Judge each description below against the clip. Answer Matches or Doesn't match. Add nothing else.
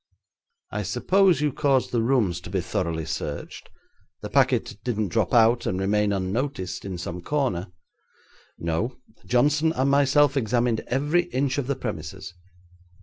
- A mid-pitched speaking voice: Doesn't match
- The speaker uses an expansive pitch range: Matches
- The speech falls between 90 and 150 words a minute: Matches